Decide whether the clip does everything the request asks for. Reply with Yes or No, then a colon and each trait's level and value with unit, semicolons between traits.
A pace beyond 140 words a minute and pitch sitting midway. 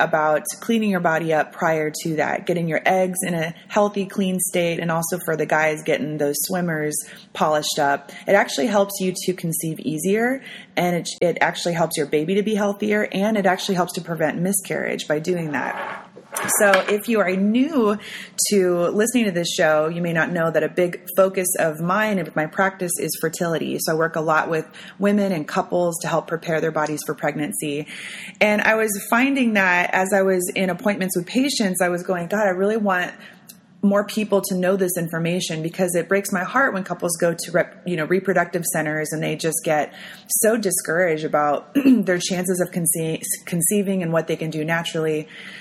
Yes: average, 200 wpm; medium, 180 Hz